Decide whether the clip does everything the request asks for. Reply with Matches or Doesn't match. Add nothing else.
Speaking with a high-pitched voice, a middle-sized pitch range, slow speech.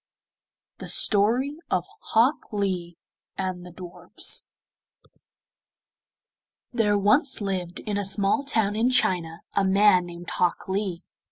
Matches